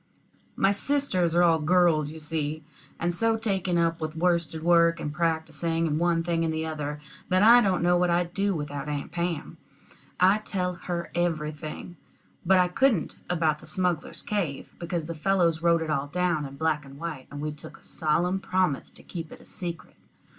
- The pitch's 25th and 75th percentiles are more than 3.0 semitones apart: No, narrow, 2.5 semitones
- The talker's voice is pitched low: No, medium, 170 Hz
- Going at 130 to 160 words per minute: No, average, 190 wpm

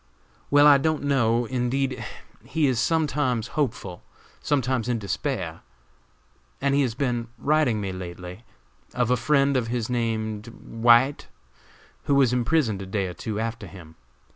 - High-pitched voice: No, low, 120 Hz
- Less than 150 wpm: Yes, average, 140 wpm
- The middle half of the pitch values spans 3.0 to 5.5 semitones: Yes, average, 3.8 semitones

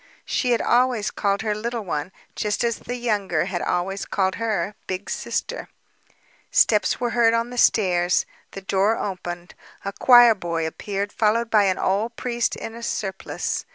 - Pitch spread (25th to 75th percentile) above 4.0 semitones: No, average, 3.6 semitones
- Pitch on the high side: Yes, high, 210 Hz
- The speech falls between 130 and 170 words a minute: Yes, average, 165 wpm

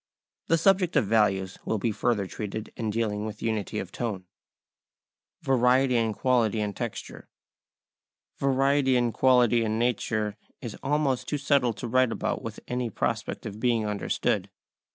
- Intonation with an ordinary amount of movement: Yes, average, 3.2 semitones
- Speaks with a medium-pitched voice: No, low, 115 Hz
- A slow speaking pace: No, average, 155 wpm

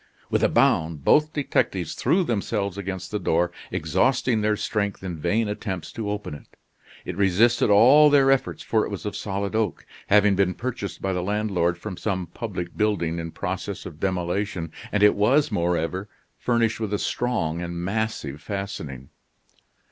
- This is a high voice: No, low, 100 Hz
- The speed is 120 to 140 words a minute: No, average, 165 wpm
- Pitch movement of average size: Yes, average, 3.9 semitones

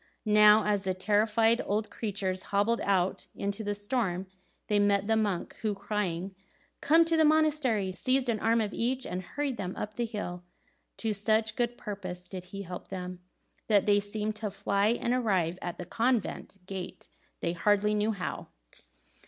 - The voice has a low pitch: No, high, 210 Hz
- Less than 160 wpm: No, average, 170 wpm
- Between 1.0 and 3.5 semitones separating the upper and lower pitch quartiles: Yes, average, 2.8 semitones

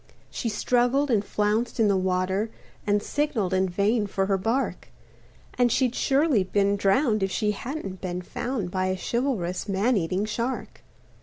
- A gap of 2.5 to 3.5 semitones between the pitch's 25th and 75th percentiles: No, average, 4.3 semitones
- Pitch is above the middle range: Yes, high, 210 Hz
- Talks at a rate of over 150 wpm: Yes, average, 160 wpm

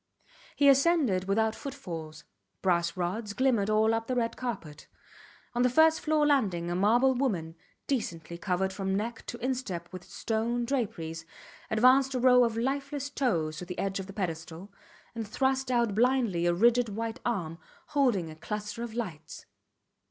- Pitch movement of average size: No, wide, 5.8 semitones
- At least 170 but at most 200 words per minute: No, average, 160 wpm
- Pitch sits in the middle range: No, high, 220 Hz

